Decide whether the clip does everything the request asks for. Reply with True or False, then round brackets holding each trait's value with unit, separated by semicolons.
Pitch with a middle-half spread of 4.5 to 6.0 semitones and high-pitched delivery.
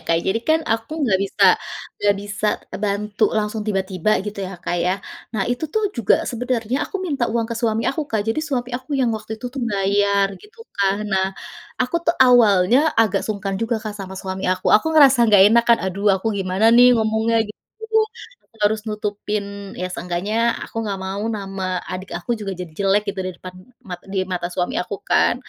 False (3.2 semitones; 210 Hz)